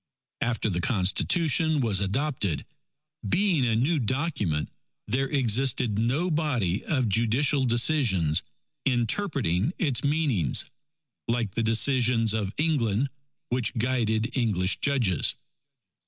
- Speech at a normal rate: No, slow, 105 wpm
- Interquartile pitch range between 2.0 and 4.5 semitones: No, average, 5.0 semitones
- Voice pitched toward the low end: Yes, low, 120 Hz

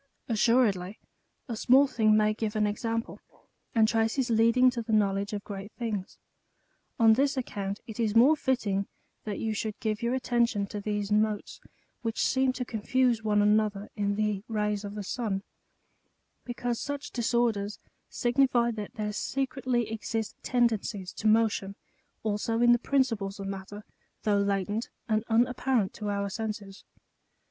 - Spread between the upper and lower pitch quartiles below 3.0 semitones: Yes, narrow, 2.6 semitones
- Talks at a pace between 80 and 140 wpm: No, average, 155 wpm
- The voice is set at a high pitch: Yes, high, 220 Hz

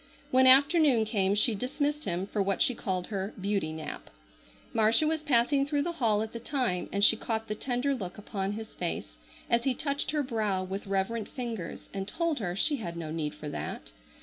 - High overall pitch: Yes, high, 220 Hz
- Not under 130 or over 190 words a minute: No, fast, 205 wpm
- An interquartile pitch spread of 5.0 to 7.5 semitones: Yes, wide, 5.4 semitones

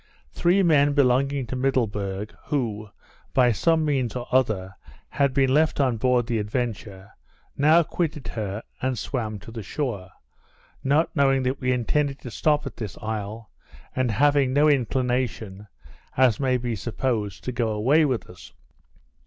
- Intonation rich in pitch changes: No, average, 4.2 semitones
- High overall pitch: No, low, 125 Hz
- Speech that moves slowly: No, average, 155 wpm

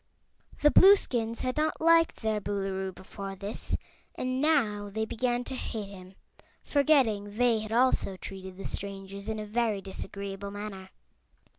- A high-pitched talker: Yes, high, 210 Hz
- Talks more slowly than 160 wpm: Yes, average, 145 wpm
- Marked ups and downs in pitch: No, average, 4.0 semitones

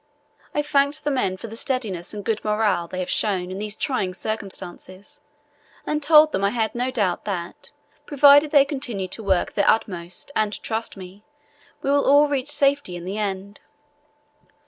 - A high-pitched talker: Yes, high, 215 Hz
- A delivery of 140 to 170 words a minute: No, average, 180 wpm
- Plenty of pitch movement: Yes, wide, 6.7 semitones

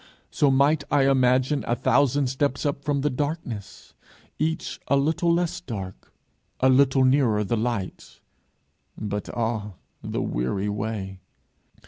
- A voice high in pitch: No, low, 130 Hz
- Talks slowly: Yes, slow, 130 wpm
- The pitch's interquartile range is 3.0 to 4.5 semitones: No, average, 4.9 semitones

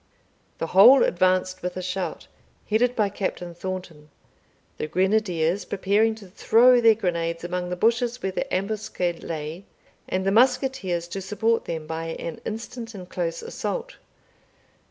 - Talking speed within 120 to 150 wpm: Yes, average, 145 wpm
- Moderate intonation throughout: Yes, average, 4.1 semitones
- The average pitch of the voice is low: No, high, 190 Hz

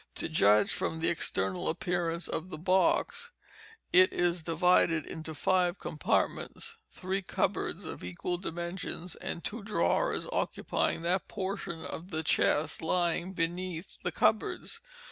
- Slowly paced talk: Yes, slow, 125 wpm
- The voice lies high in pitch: No, medium, 175 Hz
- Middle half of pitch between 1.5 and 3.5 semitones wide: Yes, narrow, 2.4 semitones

